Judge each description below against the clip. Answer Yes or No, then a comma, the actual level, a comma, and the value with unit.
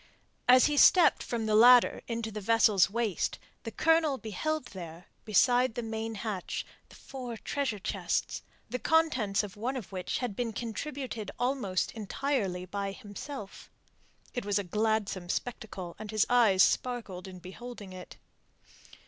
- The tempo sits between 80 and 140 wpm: No, average, 150 wpm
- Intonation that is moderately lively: Yes, average, 4.0 semitones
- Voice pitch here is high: Yes, high, 220 Hz